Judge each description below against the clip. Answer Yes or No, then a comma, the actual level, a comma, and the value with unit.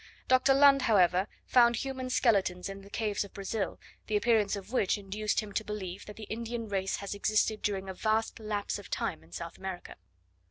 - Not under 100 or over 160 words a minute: No, average, 195 wpm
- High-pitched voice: Yes, high, 210 Hz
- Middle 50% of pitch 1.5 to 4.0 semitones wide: Yes, narrow, 2.6 semitones